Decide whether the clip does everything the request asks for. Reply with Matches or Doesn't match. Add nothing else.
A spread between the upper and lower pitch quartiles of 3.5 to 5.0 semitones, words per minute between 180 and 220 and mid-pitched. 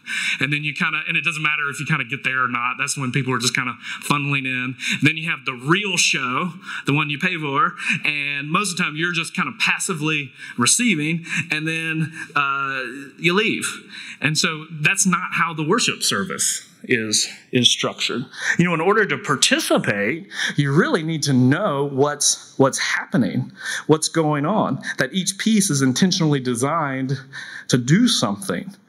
Matches